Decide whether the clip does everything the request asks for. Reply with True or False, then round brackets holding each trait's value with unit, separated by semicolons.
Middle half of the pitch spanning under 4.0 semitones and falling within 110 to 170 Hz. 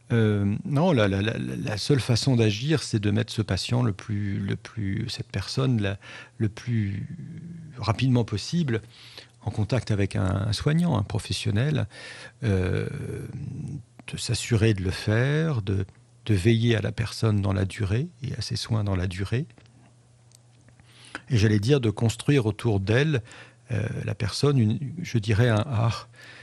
True (3.3 semitones; 115 Hz)